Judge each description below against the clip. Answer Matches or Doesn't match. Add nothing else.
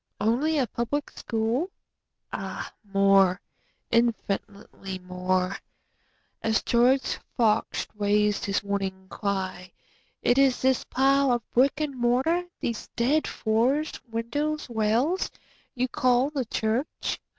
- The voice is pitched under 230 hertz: Doesn't match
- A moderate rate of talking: Doesn't match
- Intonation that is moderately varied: Matches